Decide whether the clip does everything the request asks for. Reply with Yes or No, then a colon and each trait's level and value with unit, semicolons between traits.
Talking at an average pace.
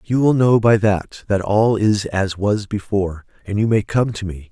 No: fast, 225 wpm